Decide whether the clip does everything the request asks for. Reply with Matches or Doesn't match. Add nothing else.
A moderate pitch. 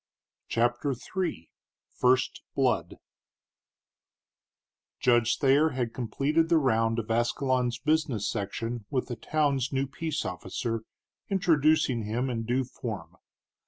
Doesn't match